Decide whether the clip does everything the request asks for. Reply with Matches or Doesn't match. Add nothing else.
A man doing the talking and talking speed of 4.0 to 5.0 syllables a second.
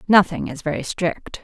Doesn't match